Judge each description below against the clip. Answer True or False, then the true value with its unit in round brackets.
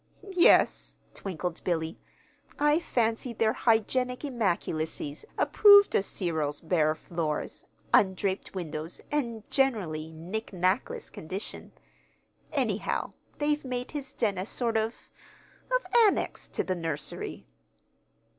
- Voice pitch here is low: False (200 Hz)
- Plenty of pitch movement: True (7.2 semitones)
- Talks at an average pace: False (110 wpm)